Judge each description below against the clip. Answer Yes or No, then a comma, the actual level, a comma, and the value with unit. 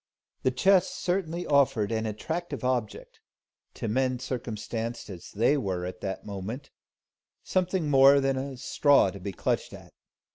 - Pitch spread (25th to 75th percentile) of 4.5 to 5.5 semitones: Yes, average, 5.2 semitones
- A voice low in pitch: Yes, low, 130 Hz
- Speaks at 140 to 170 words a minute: Yes, average, 145 wpm